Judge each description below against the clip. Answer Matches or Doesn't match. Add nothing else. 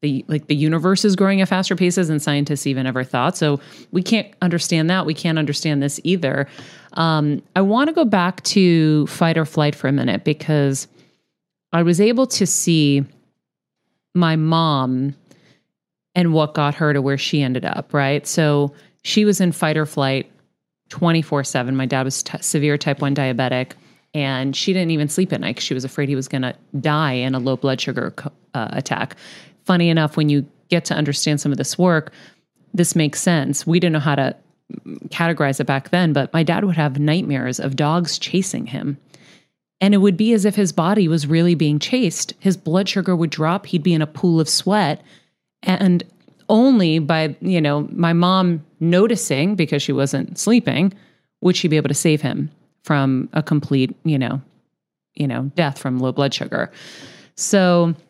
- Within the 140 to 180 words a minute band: Doesn't match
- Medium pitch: Matches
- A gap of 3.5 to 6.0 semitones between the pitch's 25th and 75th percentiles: Matches